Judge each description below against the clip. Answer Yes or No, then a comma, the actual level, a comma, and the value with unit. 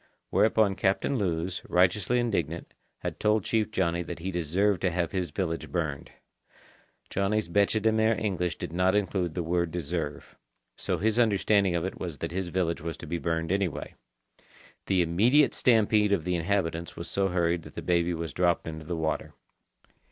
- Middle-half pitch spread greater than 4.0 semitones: No, average, 3.3 semitones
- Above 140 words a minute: Yes, average, 175 wpm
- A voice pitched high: No, very low, 90 Hz